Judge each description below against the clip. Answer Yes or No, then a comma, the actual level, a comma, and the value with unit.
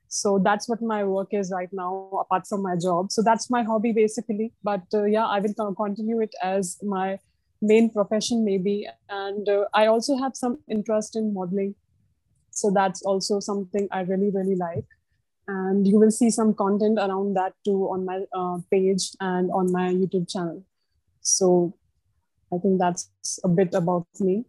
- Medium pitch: No, high, 195 Hz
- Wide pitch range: No, narrow, 2.5 semitones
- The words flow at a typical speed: Yes, average, 175 wpm